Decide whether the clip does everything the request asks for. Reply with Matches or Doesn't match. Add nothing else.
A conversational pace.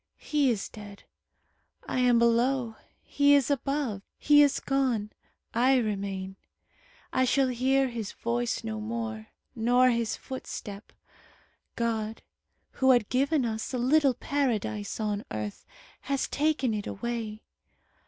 Doesn't match